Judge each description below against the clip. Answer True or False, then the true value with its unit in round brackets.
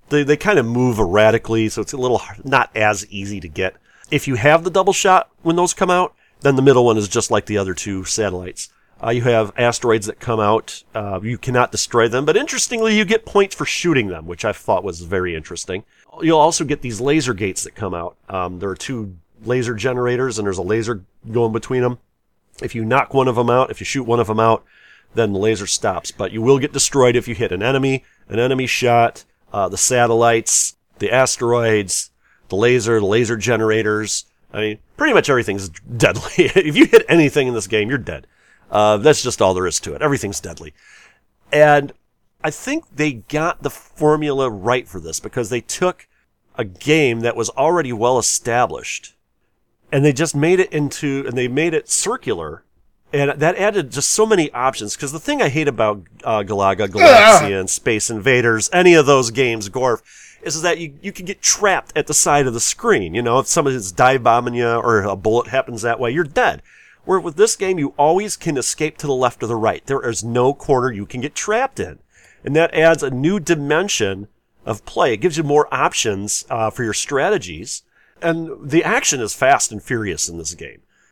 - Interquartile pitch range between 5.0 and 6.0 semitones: True (5.5 semitones)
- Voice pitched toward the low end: True (125 Hz)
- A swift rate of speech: True (210 wpm)